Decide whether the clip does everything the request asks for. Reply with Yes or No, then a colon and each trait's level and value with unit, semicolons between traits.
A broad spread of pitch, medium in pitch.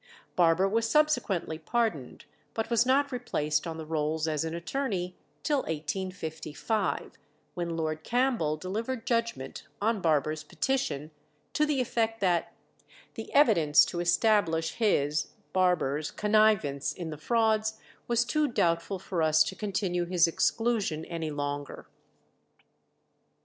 Yes: wide, 6.1 semitones; medium, 180 Hz